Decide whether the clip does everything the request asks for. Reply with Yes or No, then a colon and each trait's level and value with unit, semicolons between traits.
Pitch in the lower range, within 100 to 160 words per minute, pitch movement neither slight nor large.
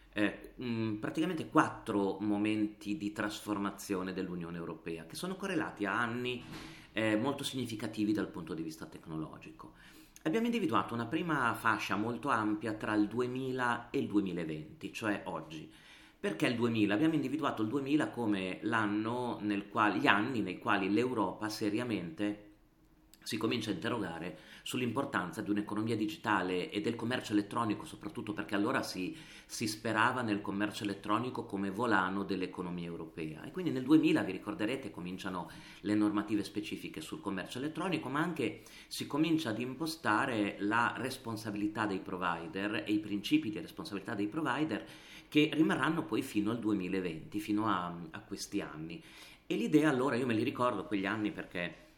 Yes: low, 105 Hz; average, 150 wpm; average, 3.3 semitones